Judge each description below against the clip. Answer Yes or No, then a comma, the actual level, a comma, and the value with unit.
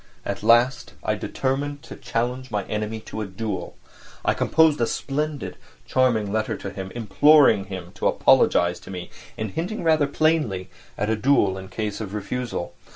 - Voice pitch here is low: Yes, low, 110 Hz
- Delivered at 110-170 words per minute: Yes, average, 165 wpm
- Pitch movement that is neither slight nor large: No, wide, 5.8 semitones